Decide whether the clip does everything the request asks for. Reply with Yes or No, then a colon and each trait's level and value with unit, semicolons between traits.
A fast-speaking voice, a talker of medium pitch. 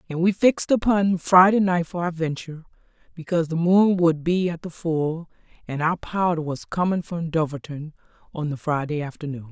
No: average, 175 wpm; medium, 165 Hz